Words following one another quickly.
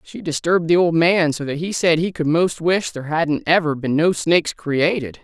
Yes: fast, 230 wpm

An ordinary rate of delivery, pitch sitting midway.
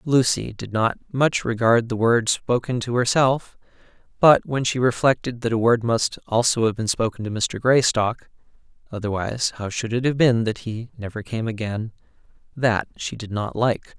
No: average, 165 wpm; low, 115 Hz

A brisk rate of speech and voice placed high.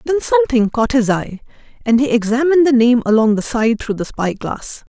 No: average, 195 wpm; high, 245 Hz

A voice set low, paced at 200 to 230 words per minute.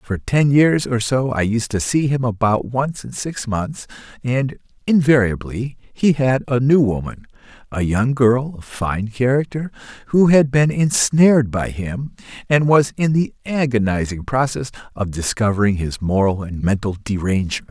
No: low, 120 Hz; average, 160 wpm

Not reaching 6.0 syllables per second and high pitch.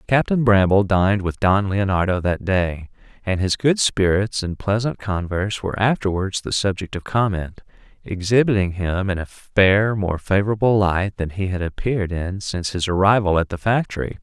No: 5.0 syllables/s; low, 100 Hz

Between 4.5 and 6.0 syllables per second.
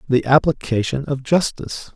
Yes: 5.0 syllables/s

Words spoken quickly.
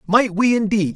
No: average, 190 wpm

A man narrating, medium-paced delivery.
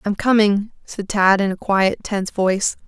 No: female; average, 190 wpm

